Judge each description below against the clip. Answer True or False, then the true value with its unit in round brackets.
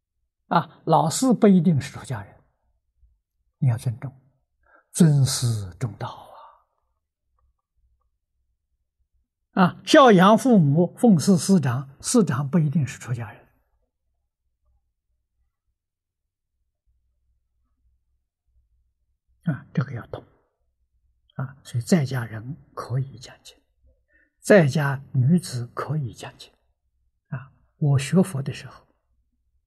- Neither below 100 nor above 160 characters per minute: True (135 characters per minute)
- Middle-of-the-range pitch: False (100 Hz)